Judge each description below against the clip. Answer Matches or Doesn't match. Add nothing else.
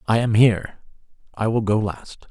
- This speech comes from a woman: Doesn't match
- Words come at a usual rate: Matches